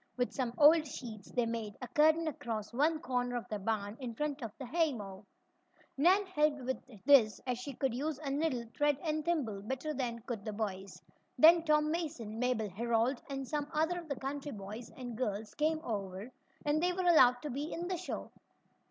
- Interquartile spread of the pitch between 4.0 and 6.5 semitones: Yes, average, 5.1 semitones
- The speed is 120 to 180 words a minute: No, average, 195 wpm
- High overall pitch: Yes, very high, 260 Hz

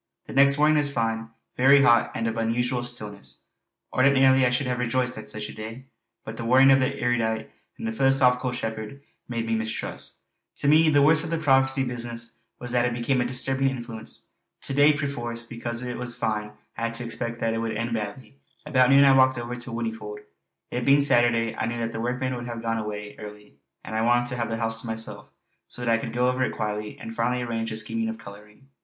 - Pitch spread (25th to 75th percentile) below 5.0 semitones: Yes, narrow, 2.6 semitones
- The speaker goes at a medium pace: No, fast, 225 wpm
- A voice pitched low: Yes, low, 120 Hz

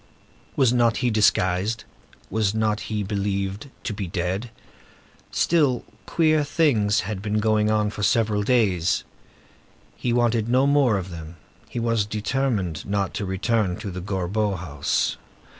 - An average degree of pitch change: Yes, average, 3.3 semitones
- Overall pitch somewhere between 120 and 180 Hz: No, low, 105 Hz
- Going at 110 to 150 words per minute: Yes, average, 140 wpm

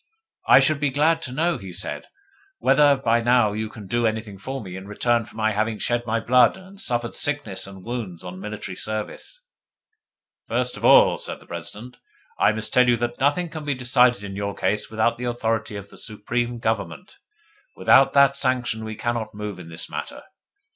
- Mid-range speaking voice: No, low, 115 Hz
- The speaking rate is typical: Yes, average, 195 wpm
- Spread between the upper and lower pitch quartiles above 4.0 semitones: No, average, 3.3 semitones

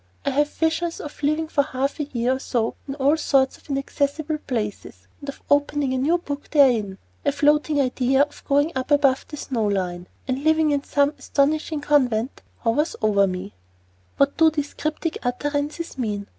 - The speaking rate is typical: Yes, average, 180 wpm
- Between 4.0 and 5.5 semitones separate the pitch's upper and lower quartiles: No, average, 2.8 semitones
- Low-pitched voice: No, very high, 280 Hz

